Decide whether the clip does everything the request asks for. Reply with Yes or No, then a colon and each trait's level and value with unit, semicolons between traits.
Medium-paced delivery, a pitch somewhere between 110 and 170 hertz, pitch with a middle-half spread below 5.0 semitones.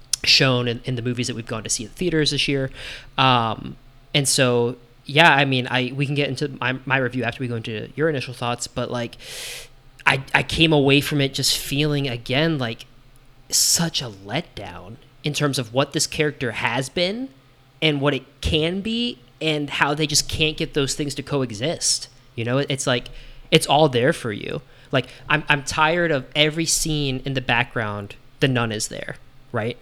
Yes: average, 195 wpm; low, 135 Hz; average, 3.3 semitones